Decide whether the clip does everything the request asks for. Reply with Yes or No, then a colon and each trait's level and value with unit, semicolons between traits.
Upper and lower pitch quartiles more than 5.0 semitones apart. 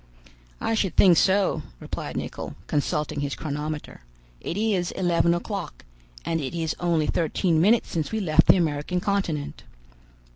No: average, 3.8 semitones